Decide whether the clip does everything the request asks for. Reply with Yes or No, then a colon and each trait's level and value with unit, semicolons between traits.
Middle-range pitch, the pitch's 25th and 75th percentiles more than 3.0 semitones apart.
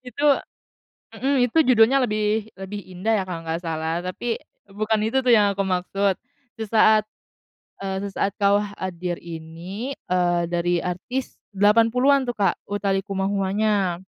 No: high, 200 Hz; average, 3.6 semitones